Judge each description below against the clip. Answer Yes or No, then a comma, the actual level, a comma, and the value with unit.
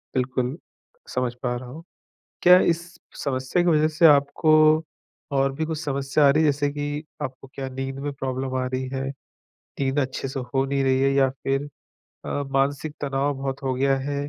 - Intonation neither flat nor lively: No, narrow, 1.7 semitones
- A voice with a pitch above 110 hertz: Yes, low, 135 Hz